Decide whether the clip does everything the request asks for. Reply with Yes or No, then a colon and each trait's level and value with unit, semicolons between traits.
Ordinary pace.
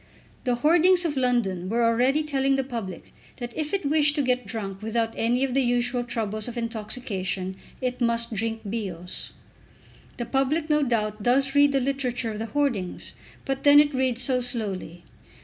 Yes: average, 175 wpm